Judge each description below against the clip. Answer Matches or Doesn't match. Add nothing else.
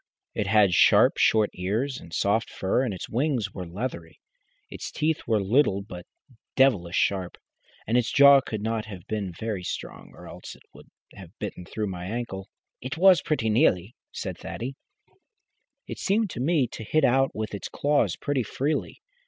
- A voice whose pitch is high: Doesn't match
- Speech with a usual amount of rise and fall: Doesn't match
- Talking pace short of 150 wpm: Doesn't match